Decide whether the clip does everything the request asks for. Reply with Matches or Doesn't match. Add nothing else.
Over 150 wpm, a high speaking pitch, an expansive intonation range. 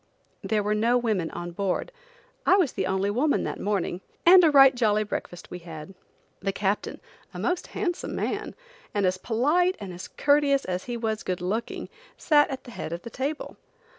Matches